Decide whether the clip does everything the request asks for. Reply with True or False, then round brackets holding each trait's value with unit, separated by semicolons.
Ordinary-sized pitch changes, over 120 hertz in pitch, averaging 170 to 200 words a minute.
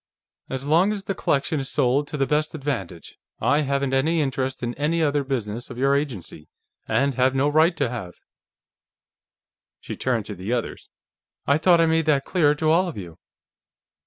True (3.5 semitones; 140 Hz; 185 wpm)